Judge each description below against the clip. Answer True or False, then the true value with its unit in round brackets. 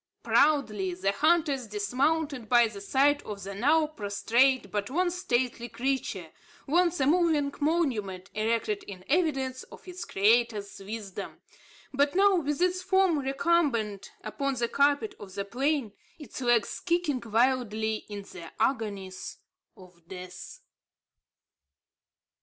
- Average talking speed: False (125 wpm)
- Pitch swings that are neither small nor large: False (6.5 semitones)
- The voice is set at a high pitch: True (250 Hz)